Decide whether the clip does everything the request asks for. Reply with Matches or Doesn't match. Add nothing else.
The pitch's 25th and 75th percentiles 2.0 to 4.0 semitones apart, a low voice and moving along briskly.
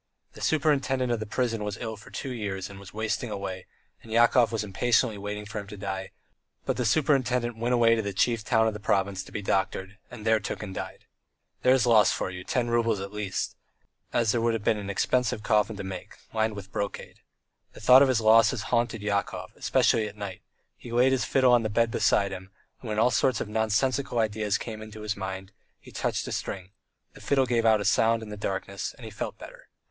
Matches